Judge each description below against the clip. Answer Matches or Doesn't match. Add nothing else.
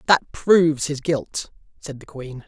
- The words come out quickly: Doesn't match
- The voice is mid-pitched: Matches